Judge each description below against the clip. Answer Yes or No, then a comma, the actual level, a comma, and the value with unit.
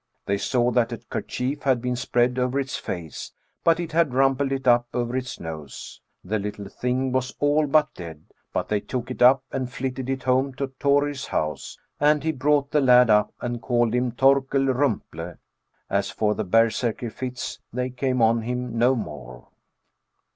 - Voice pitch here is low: Yes, low, 125 Hz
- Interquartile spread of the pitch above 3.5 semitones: No, average, 2.8 semitones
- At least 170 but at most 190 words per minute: Yes, average, 175 wpm